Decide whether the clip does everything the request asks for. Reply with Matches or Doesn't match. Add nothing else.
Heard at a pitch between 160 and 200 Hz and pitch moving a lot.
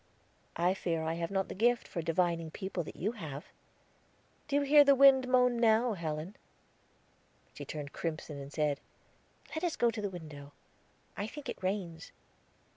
Matches